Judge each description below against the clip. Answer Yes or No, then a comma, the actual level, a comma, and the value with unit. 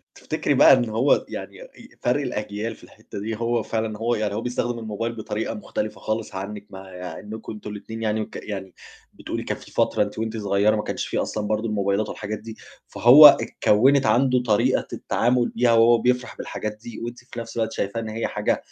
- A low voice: Yes, low, 110 Hz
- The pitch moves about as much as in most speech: No, narrow, 2.0 semitones